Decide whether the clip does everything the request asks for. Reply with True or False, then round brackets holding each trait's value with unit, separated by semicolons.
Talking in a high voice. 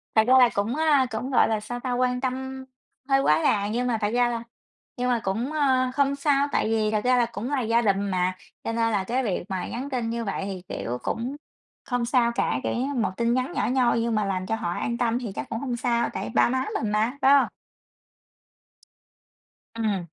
True (235 Hz)